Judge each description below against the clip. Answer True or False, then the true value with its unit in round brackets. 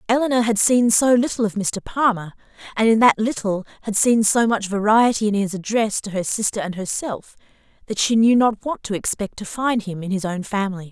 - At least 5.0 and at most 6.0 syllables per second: True (5.5 syllables/s)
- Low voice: False (215 Hz)